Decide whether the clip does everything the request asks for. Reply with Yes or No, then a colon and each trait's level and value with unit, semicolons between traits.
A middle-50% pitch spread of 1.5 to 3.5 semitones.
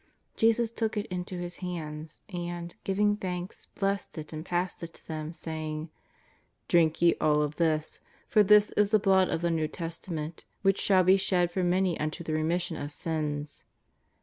Yes: average, 3.2 semitones